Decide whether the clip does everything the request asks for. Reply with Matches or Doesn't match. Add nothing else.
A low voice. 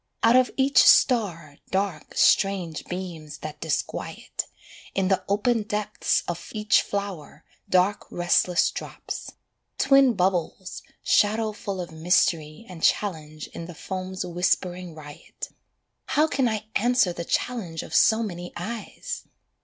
Doesn't match